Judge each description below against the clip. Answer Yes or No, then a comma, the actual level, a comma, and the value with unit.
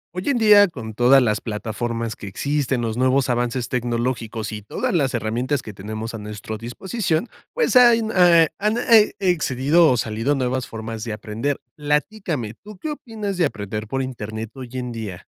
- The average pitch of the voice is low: Yes, low, 125 Hz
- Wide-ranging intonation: Yes, wide, 7.2 semitones